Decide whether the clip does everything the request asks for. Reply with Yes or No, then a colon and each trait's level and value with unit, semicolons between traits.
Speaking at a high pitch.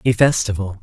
No: low, 110 Hz